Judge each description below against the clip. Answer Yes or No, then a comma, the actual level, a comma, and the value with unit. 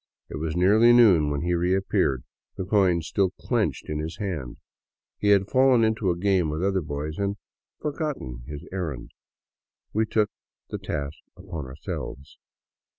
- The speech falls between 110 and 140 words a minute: No, average, 160 wpm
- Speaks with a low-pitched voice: Yes, very low, 90 Hz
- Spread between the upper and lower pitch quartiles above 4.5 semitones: Yes, average, 5.1 semitones